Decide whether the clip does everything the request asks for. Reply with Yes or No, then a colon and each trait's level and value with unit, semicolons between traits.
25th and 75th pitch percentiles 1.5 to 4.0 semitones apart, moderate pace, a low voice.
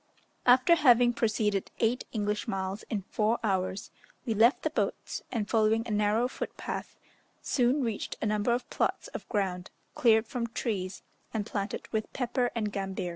No: average, 2.8 semitones; average, 160 wpm; high, 220 Hz